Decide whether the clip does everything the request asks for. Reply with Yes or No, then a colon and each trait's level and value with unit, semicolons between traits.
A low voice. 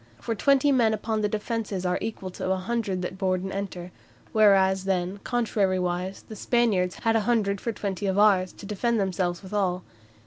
No: high, 195 Hz